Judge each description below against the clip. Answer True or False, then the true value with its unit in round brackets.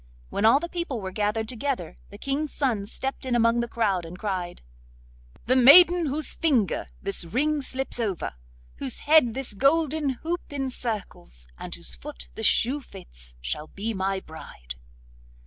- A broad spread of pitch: True (6.5 semitones)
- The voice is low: False (230 Hz)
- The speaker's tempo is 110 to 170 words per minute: True (160 wpm)